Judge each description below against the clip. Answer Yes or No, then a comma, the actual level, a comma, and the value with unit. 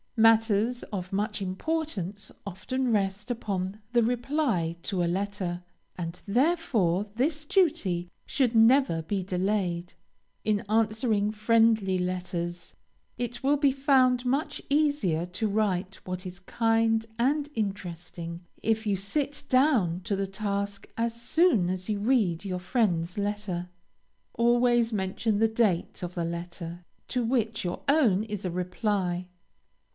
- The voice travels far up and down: No, average, 4.8 semitones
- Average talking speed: No, slow, 130 wpm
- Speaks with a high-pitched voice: Yes, high, 210 Hz